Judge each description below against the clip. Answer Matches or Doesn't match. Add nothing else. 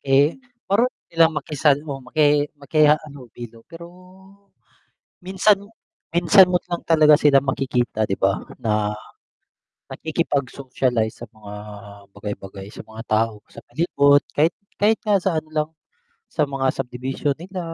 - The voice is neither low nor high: Matches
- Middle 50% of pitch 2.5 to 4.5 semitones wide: Doesn't match